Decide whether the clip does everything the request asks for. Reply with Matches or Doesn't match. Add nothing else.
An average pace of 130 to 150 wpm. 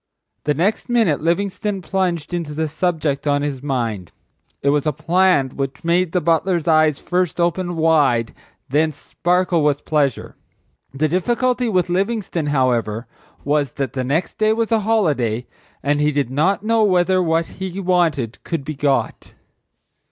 Doesn't match